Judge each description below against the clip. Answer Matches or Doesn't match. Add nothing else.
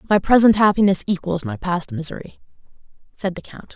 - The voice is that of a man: Doesn't match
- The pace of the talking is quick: Doesn't match